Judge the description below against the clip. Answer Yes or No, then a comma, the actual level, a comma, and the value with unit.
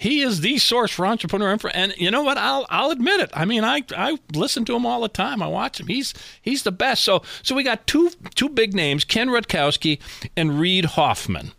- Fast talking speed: Yes, fast, 235 wpm